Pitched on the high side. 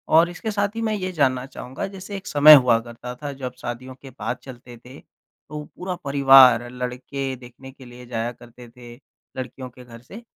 No: low, 130 Hz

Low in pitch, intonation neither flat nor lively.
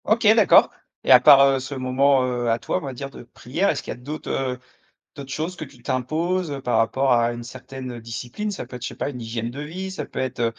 Yes: low, 130 Hz; average, 3.3 semitones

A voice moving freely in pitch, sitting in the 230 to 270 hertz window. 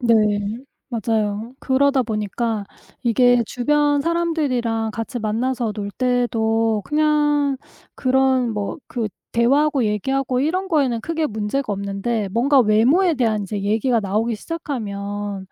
No: average, 4.4 semitones; high, 240 Hz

